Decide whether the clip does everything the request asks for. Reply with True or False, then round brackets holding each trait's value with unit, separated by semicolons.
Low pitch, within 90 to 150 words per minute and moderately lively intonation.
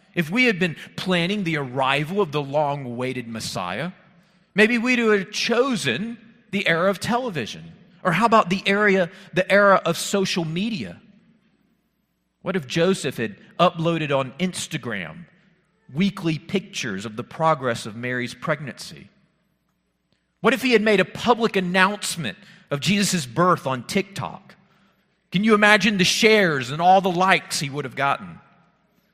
False (185 Hz; 145 wpm; 4.0 semitones)